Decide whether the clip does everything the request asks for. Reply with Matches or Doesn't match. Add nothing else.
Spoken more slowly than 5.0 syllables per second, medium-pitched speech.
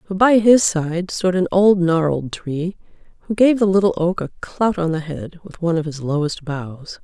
Matches